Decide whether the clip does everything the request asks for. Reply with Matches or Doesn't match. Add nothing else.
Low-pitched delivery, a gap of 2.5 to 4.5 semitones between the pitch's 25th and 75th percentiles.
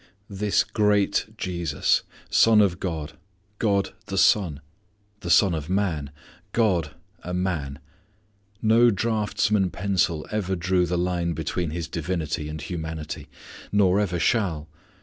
Matches